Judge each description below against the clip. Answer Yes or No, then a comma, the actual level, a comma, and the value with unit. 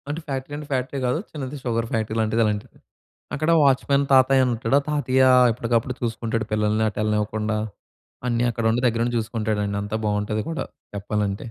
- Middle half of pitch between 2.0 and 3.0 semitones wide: No, average, 3.4 semitones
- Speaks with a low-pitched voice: Yes, low, 115 Hz